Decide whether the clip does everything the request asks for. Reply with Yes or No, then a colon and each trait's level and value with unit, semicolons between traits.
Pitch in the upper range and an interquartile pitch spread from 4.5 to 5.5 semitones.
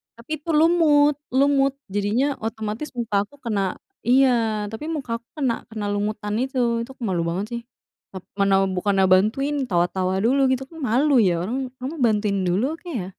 Yes: high, 230 Hz; average, 5.0 semitones